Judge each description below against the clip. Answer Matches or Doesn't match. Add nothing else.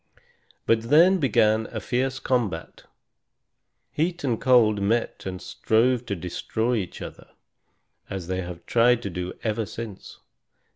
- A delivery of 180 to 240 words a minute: Doesn't match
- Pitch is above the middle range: Doesn't match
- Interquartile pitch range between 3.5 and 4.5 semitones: Matches